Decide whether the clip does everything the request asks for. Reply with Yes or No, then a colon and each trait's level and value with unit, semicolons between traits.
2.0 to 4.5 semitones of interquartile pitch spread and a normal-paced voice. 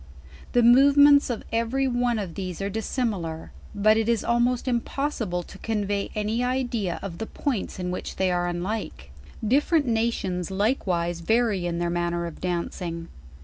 No: wide, 5.4 semitones; average, 160 wpm